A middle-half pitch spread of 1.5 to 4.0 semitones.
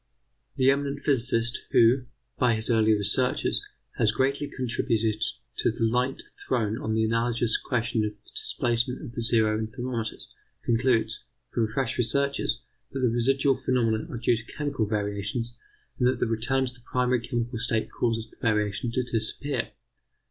Yes: narrow, 2.4 semitones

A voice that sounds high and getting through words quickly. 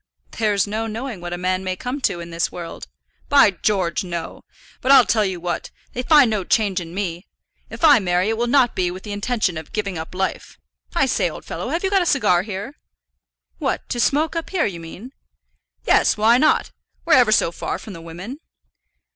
Yes: high, 205 Hz; fast, 215 wpm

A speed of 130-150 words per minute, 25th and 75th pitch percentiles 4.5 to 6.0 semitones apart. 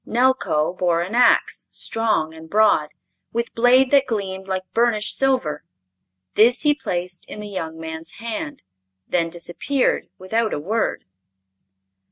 Yes: slow, 135 wpm; wide, 5.5 semitones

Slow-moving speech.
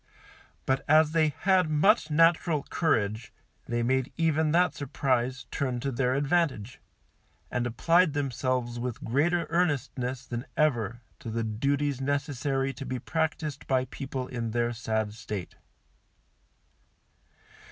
Yes: slow, 125 wpm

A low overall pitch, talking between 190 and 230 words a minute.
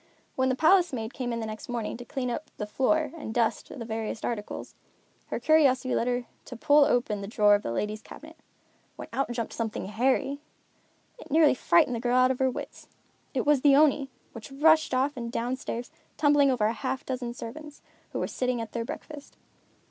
No: very high, 250 Hz; average, 200 wpm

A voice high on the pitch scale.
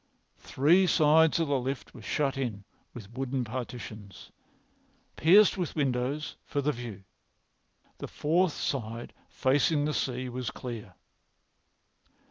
No: low, 130 Hz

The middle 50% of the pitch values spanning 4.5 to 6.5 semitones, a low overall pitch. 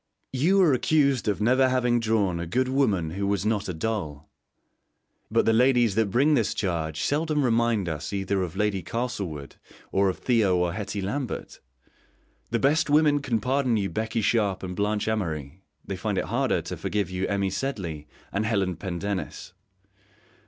Yes: average, 5.1 semitones; low, 105 Hz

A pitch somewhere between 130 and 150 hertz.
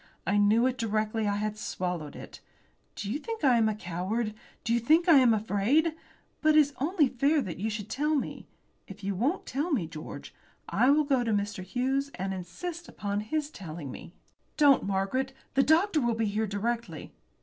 No: high, 230 Hz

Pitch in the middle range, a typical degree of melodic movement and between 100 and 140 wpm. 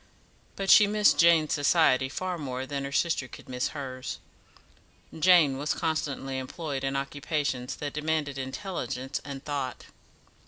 Yes: medium, 145 Hz; average, 3.1 semitones; slow, 135 wpm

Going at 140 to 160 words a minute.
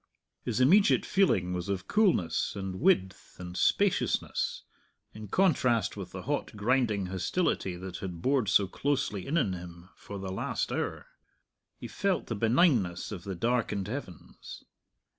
Yes: average, 145 wpm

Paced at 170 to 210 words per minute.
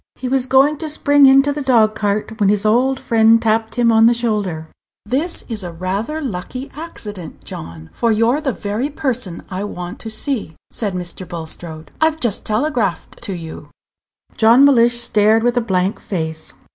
Yes: average, 175 wpm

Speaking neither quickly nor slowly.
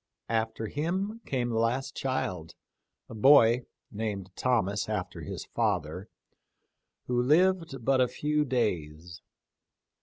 No: slow, 125 wpm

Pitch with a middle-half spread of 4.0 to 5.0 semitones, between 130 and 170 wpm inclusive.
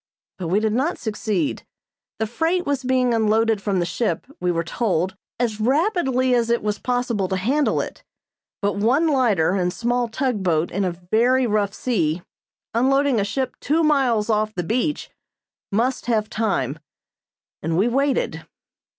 Yes: average, 4.6 semitones; average, 160 wpm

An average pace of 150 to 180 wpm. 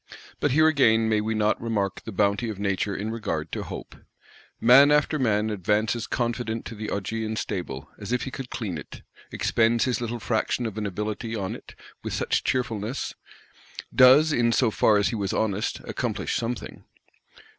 Yes: average, 175 wpm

